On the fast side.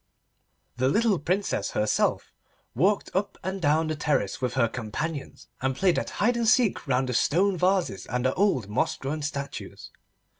No: average, 165 wpm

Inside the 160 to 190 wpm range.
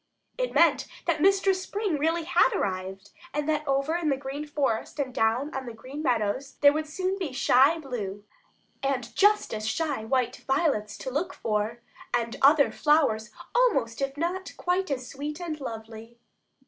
Yes: average, 170 wpm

